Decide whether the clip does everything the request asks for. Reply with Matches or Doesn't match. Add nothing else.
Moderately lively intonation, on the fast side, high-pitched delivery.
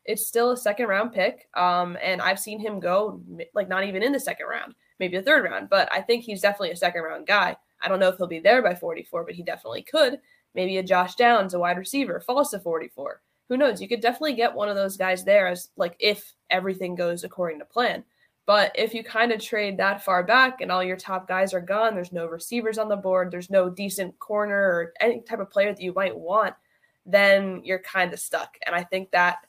Matches